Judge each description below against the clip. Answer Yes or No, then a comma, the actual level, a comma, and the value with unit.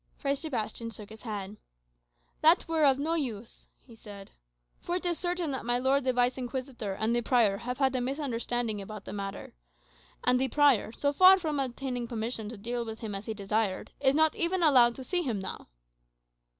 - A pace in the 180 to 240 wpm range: Yes, average, 200 wpm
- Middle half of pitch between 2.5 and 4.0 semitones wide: No, average, 4.4 semitones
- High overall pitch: Yes, high, 245 Hz